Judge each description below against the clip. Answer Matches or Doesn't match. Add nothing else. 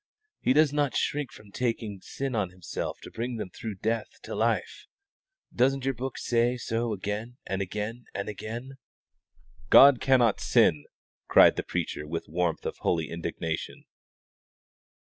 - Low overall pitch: Matches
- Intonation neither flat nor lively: Matches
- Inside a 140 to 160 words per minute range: Matches